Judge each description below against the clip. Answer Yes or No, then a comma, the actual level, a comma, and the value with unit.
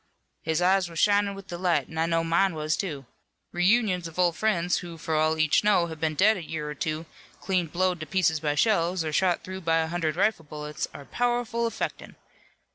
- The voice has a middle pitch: Yes, medium, 170 Hz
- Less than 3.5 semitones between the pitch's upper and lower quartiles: Yes, average, 3.1 semitones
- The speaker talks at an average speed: No, fast, 210 wpm